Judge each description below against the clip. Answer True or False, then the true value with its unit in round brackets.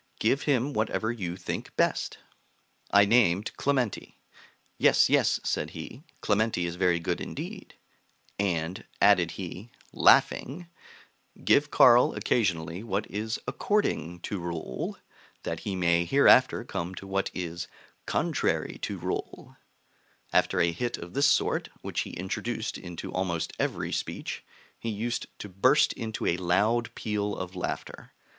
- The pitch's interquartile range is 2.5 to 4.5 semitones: False (4.9 semitones)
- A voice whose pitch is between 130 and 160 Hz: False (100 Hz)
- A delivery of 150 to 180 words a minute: False (135 wpm)